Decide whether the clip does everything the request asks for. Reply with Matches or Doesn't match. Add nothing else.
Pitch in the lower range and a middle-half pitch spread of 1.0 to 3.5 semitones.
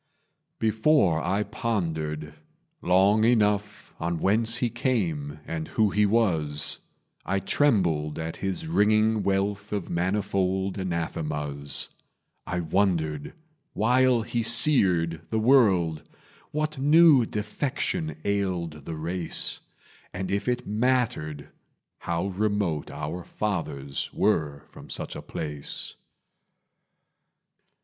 Doesn't match